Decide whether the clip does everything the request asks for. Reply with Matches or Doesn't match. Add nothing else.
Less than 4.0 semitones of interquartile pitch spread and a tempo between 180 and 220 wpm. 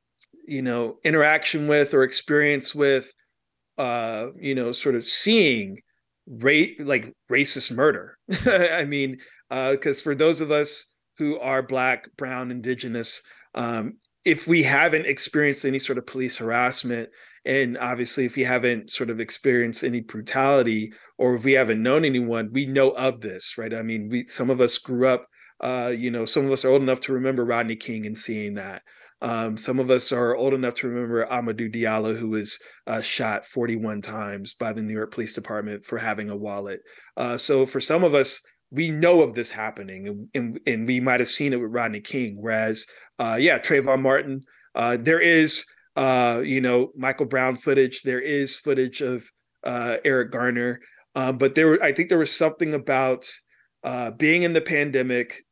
Matches